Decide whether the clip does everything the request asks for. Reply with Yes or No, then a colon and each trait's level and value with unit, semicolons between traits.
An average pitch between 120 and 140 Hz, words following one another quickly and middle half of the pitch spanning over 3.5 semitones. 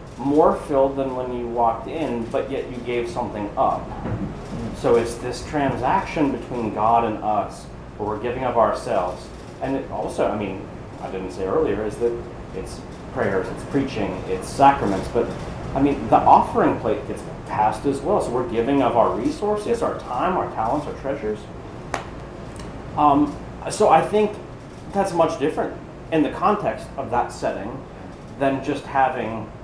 No: low, 135 Hz; average, 165 wpm; average, 4.1 semitones